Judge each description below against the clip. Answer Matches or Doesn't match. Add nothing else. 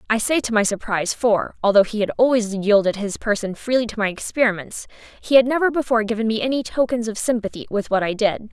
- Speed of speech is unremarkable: Doesn't match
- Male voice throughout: Doesn't match